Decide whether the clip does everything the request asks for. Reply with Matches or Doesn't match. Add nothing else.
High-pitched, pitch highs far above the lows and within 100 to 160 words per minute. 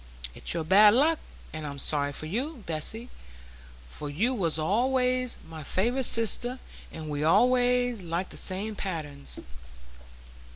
Matches